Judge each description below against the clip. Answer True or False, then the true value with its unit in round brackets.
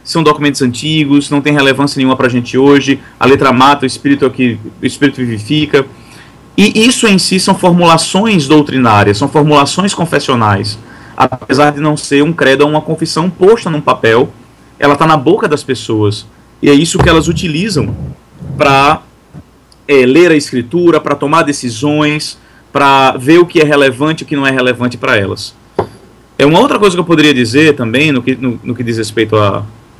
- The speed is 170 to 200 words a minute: True (185 wpm)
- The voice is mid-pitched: True (145 Hz)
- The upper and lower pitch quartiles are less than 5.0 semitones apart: True (3.3 semitones)